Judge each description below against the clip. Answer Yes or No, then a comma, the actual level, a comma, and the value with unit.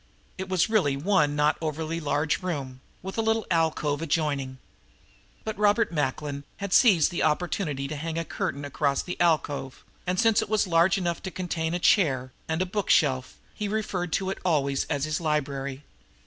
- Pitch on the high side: No, medium, 160 Hz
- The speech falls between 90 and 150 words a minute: No, average, 175 wpm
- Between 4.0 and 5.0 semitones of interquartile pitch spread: Yes, average, 4.5 semitones